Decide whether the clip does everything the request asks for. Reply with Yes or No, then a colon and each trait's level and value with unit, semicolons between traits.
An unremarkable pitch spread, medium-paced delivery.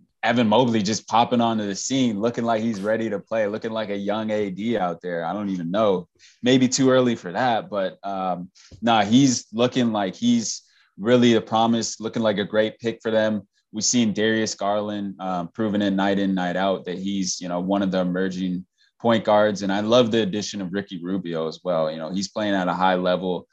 No: average, 3.3 semitones; fast, 215 wpm